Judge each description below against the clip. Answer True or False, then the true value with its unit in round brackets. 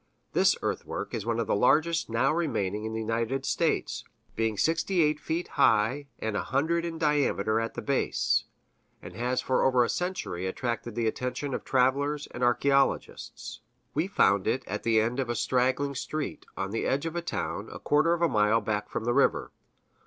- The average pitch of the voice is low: True (125 Hz)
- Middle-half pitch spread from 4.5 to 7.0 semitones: True (4.8 semitones)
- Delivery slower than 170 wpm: False (190 wpm)